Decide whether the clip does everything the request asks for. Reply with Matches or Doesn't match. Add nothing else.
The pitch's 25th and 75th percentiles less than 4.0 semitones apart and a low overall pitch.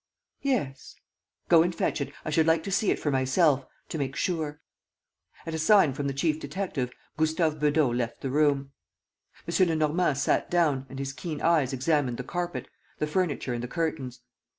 Doesn't match